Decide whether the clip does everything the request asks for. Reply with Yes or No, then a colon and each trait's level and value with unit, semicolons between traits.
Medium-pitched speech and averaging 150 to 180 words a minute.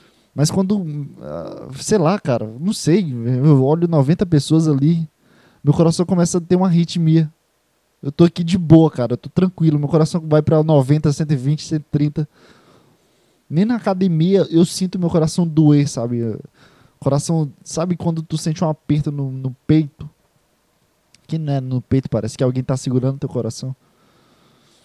Yes: medium, 155 Hz; average, 160 wpm